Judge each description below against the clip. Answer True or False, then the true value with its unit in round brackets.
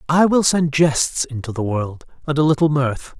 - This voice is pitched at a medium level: True (145 Hz)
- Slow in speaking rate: False (205 wpm)